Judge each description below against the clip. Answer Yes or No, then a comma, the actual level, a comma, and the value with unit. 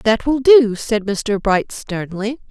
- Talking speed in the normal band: Yes, average, 170 wpm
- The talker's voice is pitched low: No, high, 225 Hz